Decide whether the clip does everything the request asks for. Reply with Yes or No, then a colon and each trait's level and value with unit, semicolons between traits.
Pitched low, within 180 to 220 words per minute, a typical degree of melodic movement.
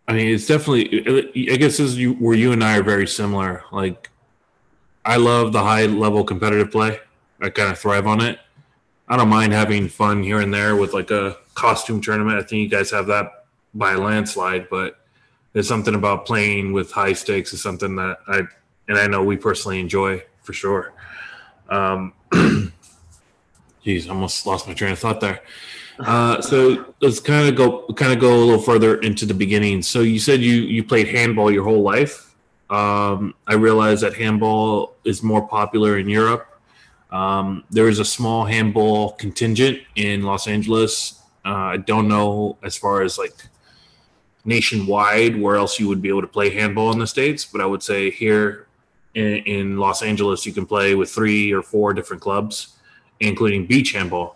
No: low, 105 Hz; average, 185 wpm; narrow, 2.0 semitones